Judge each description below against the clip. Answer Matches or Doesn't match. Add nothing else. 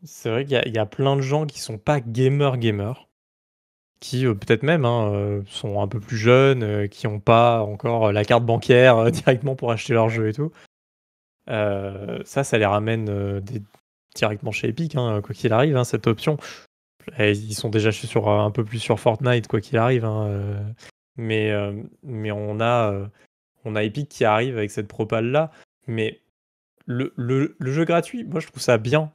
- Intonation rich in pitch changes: Doesn't match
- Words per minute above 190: Matches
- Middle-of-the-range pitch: Doesn't match